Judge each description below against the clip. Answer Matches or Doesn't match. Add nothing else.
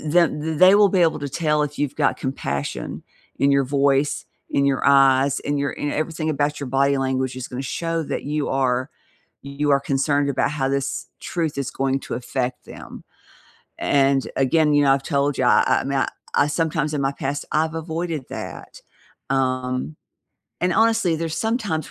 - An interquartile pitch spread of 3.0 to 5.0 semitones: Doesn't match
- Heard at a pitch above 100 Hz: Matches